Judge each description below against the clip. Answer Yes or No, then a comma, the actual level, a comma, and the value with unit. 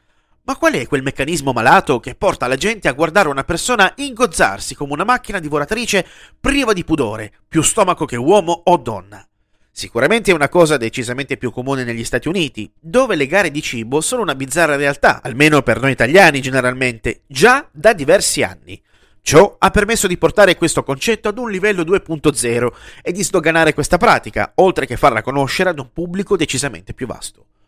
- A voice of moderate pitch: Yes, medium, 155 Hz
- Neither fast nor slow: No, fast, 180 wpm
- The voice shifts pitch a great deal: Yes, wide, 6.3 semitones